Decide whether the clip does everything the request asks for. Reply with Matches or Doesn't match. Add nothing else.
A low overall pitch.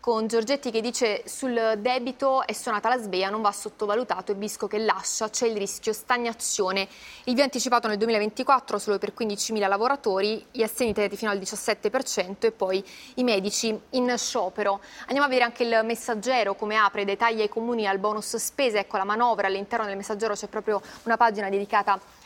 Doesn't match